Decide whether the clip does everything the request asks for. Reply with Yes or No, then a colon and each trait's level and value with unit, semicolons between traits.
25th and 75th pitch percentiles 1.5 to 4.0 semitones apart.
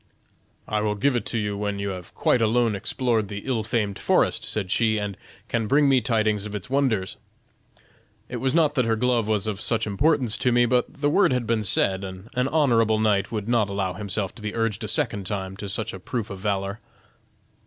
Yes: average, 3.3 semitones